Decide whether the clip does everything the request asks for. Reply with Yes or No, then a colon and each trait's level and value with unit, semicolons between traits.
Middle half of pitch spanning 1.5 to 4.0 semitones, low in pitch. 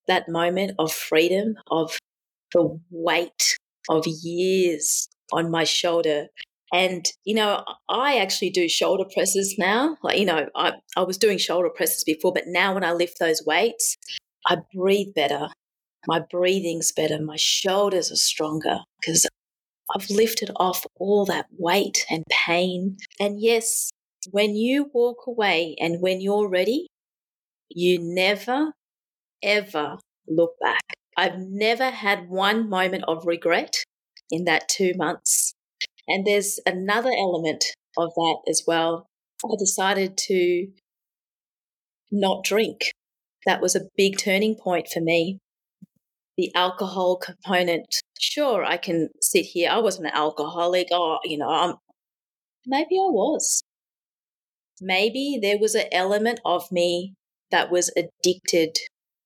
No: average, 3.3 semitones; medium, 185 Hz